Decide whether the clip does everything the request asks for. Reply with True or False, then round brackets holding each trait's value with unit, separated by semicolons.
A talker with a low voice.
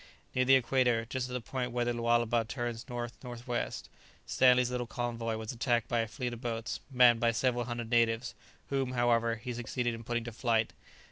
True (120 Hz)